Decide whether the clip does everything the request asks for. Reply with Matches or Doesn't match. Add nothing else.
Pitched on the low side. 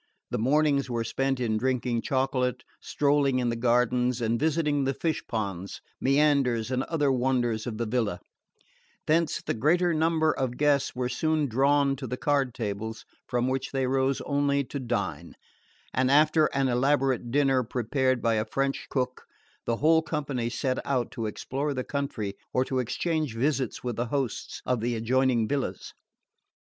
Matches